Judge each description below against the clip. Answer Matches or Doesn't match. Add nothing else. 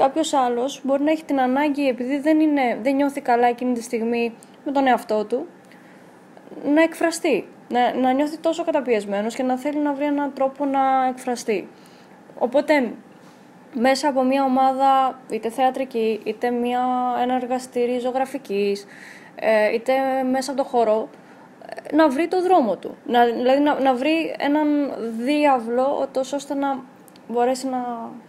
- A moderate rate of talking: Matches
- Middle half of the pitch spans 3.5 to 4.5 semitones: Doesn't match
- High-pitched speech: Matches